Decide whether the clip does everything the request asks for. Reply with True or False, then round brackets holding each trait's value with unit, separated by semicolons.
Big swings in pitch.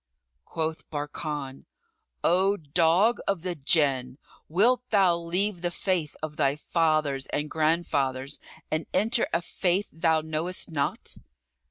False (3.5 semitones)